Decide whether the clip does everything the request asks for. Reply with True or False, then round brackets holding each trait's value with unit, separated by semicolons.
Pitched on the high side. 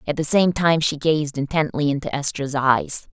False (150 Hz)